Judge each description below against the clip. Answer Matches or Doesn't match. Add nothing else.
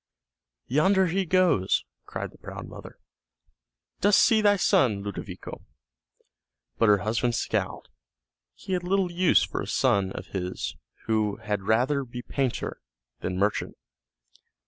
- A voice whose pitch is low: Matches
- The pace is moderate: Doesn't match